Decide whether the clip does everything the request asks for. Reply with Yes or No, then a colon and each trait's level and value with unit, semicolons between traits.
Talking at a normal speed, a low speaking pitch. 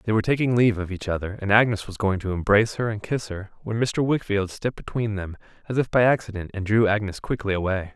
No: fast, 240 wpm; low, 105 Hz